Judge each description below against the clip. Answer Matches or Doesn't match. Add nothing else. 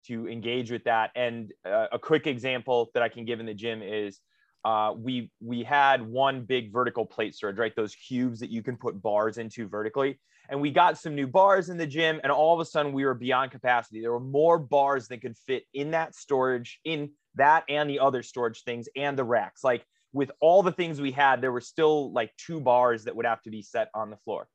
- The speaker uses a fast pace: Matches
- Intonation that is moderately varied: Matches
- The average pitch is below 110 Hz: Doesn't match